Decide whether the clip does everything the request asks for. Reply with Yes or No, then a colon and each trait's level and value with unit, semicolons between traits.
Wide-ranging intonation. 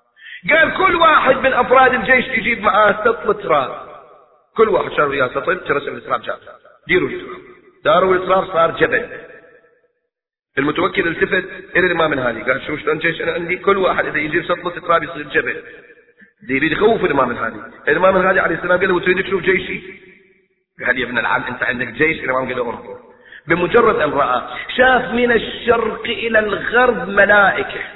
Yes: wide, 6.5 semitones